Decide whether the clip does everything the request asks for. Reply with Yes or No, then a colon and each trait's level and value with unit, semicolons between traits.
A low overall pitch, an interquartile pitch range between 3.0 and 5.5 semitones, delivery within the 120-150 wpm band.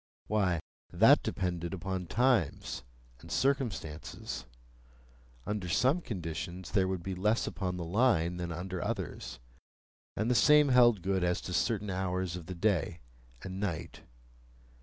Yes: very low, 95 Hz; average, 3.5 semitones; average, 140 wpm